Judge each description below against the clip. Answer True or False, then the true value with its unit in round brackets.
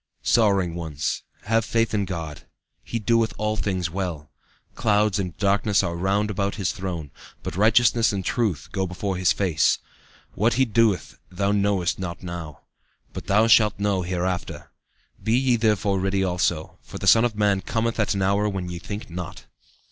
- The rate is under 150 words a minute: False (170 wpm)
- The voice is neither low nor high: False (100 Hz)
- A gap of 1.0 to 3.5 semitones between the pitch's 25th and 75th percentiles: True (3.1 semitones)